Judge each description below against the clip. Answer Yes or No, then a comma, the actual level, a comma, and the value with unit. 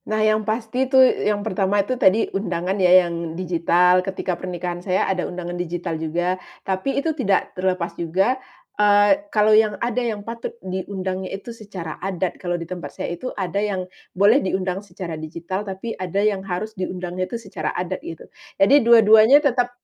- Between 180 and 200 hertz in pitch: Yes, high, 190 Hz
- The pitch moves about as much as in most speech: Yes, average, 3.3 semitones